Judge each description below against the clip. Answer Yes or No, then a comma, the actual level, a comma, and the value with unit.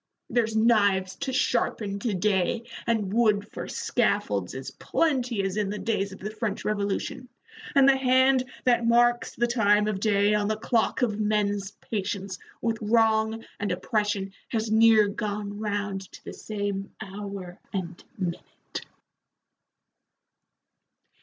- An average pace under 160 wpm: Yes, average, 140 wpm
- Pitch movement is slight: Yes, narrow, 2.3 semitones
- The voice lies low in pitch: No, high, 210 Hz